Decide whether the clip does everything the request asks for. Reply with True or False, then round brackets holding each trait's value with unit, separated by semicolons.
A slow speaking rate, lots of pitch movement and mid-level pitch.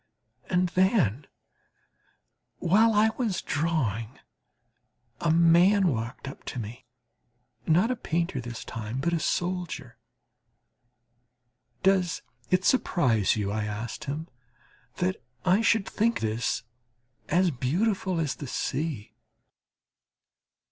True (105 wpm; 7.2 semitones; 165 Hz)